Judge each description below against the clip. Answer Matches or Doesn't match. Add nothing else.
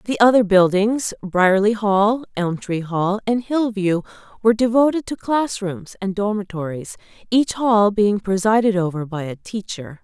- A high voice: Matches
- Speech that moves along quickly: Doesn't match